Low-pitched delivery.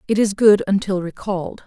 No: high, 195 Hz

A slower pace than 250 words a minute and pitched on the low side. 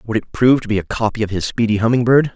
No: fast, 305 wpm; low, 115 Hz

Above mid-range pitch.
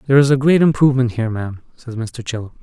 No: low, 125 Hz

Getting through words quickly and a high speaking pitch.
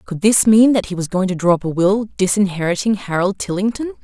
Yes: fast, 225 wpm; high, 195 Hz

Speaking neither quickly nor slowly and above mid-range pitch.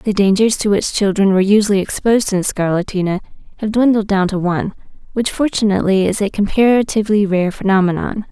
Yes: average, 160 wpm; high, 205 Hz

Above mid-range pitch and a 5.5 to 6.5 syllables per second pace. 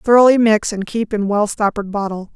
Yes: high, 210 Hz; 5.6 syllables/s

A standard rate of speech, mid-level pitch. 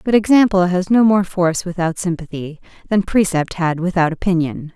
Yes: average, 165 wpm; medium, 180 Hz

